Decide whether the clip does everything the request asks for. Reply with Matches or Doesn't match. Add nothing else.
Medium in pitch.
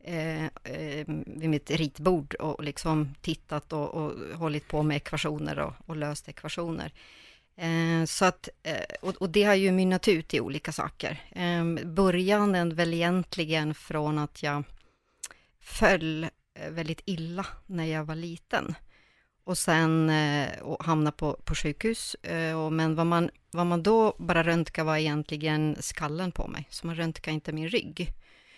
Matches